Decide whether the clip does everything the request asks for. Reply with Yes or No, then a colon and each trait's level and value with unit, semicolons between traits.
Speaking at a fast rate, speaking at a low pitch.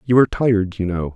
Yes: fast, 260 wpm; low, 105 Hz